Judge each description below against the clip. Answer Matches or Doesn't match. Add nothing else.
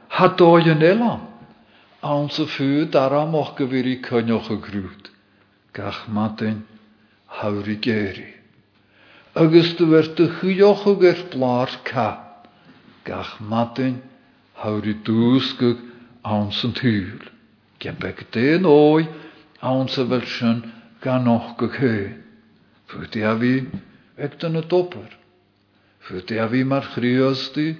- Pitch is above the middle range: Doesn't match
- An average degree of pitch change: Doesn't match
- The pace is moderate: Doesn't match